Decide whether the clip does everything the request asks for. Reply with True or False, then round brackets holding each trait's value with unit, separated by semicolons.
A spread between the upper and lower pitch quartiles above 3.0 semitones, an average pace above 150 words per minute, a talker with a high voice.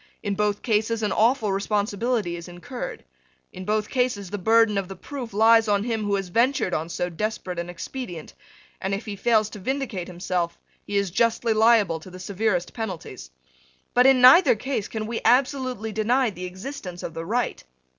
True (4.0 semitones; 185 wpm; 210 Hz)